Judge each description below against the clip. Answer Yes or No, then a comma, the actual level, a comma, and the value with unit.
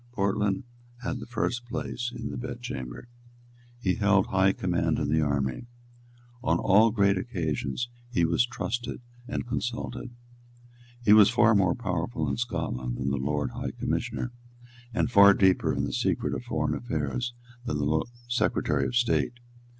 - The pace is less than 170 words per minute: Yes, average, 155 wpm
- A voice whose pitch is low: Yes, low, 100 Hz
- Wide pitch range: Yes, wide, 7.3 semitones